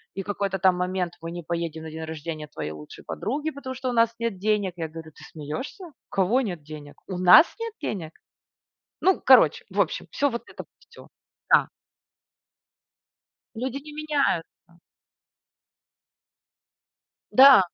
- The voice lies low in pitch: No, high, 190 Hz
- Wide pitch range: Yes, wide, 8.1 semitones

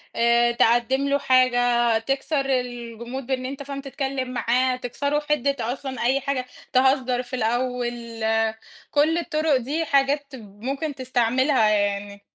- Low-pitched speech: No, very high, 255 Hz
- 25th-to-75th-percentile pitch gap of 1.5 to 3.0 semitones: Yes, narrow, 2.6 semitones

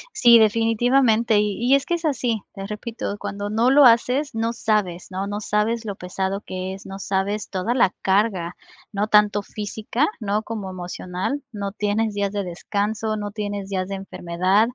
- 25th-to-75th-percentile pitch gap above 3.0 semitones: No, narrow, 2.6 semitones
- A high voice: Yes, high, 210 Hz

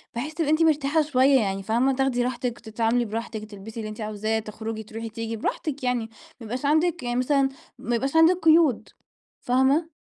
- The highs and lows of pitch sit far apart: No, average, 4.1 semitones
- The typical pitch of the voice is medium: No, high, 245 Hz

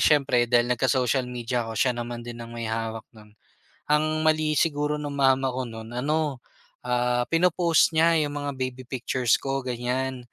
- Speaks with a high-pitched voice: No, low, 130 Hz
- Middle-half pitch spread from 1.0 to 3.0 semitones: No, average, 3.5 semitones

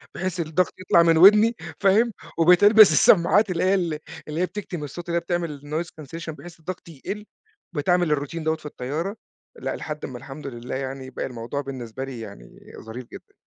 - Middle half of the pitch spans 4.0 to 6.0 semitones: Yes, average, 4.7 semitones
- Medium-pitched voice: Yes, medium, 160 Hz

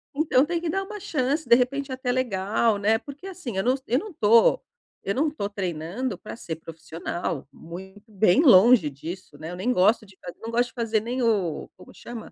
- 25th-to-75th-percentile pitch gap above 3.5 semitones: Yes, wide, 5.5 semitones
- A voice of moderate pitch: No, high, 225 Hz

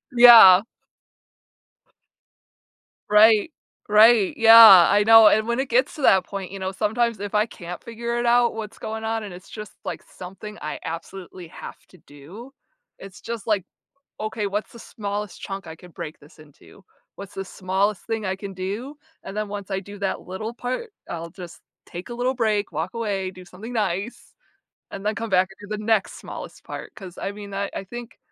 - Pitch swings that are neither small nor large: Yes, average, 3.1 semitones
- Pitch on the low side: No, high, 205 Hz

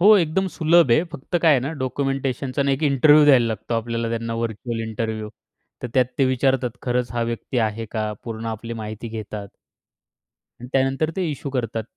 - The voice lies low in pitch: Yes, low, 125 Hz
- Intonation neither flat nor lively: Yes, average, 3.3 semitones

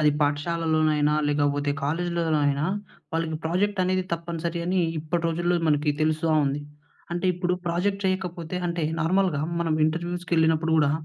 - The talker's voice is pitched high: No, medium, 165 Hz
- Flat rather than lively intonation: Yes, narrow, 2.3 semitones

